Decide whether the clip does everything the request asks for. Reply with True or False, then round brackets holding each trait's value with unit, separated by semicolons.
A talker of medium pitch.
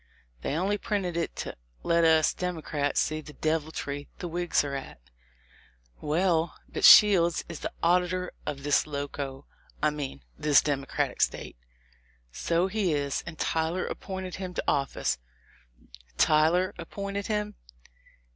True (165 Hz)